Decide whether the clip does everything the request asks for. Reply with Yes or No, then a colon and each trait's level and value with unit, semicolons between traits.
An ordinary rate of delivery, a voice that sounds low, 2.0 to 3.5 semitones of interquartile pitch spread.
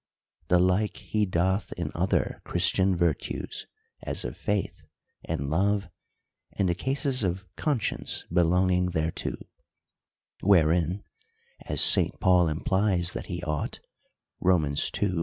No: slow, 120 wpm; very low, 90 Hz; narrow, 2.6 semitones